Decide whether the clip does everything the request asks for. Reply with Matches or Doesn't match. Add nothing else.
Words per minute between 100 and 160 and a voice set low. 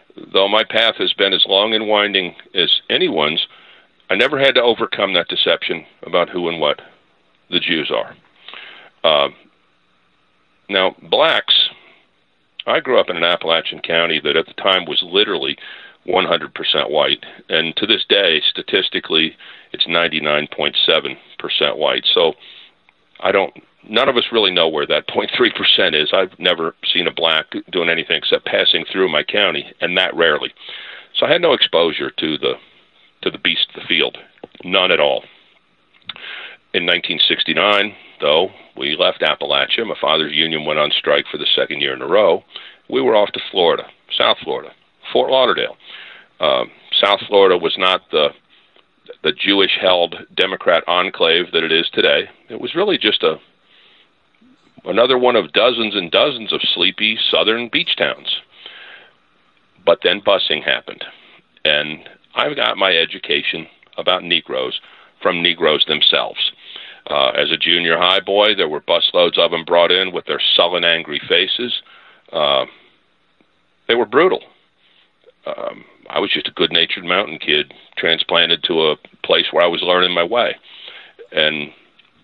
Matches